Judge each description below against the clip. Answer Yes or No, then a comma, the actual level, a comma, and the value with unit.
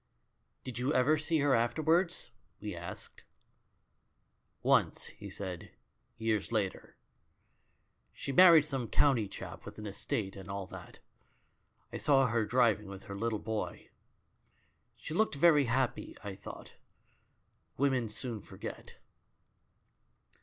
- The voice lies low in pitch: Yes, low, 115 Hz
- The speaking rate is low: Yes, slow, 125 wpm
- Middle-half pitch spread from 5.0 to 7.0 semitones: Yes, average, 5.3 semitones